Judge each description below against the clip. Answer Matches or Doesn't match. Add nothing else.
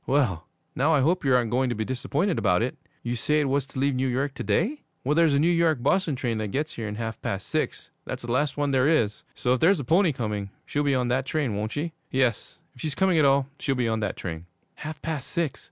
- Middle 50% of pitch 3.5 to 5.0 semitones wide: Matches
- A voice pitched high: Doesn't match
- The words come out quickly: Matches